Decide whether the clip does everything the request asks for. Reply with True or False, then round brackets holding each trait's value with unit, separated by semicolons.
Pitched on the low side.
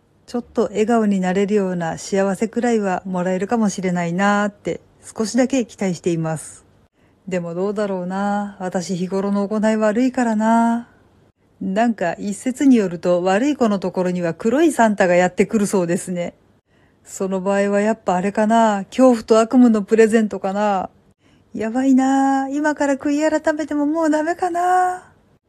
False (210 Hz)